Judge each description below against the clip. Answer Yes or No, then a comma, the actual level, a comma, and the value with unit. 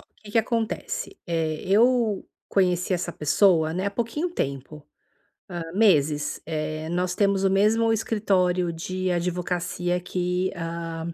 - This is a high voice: No, medium, 180 Hz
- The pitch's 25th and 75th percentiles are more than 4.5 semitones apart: No, average, 3.6 semitones